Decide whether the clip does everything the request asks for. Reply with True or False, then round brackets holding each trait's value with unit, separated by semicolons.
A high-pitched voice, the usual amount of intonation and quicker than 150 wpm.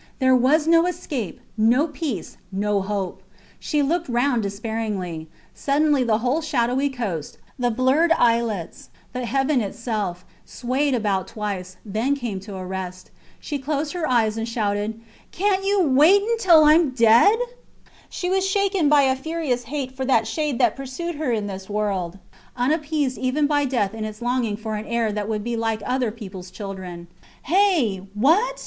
False (245 Hz; 5.9 semitones; 165 wpm)